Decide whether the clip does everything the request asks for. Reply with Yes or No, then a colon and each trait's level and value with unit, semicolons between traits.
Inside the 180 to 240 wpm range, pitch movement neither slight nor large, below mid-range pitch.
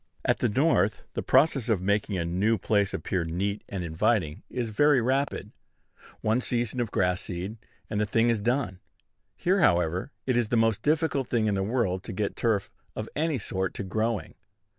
Yes: average, 185 wpm; average, 4.1 semitones; low, 110 Hz